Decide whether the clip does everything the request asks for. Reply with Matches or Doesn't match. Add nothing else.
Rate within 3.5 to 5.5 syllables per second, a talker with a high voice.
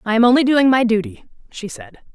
Doesn't match